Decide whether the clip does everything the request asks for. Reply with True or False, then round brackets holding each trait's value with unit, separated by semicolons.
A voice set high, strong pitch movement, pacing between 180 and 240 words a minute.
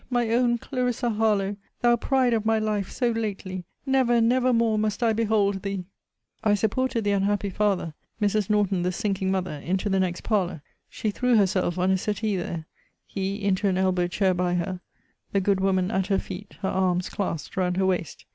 False (200 Hz; 2.9 semitones; 190 wpm)